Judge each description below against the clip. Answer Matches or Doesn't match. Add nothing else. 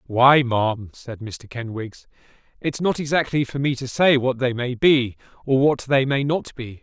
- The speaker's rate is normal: Matches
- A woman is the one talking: Doesn't match